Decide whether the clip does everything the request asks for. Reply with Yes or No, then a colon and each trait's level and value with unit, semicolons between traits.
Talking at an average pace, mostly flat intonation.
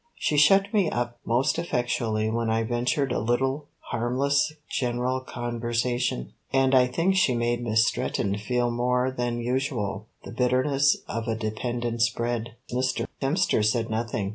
Yes: average, 145 wpm; narrow, 2.1 semitones